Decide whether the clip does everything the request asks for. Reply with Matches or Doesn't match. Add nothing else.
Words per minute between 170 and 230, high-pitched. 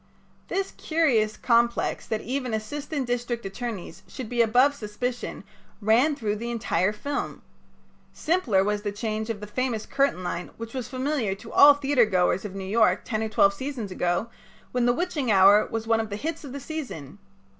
Matches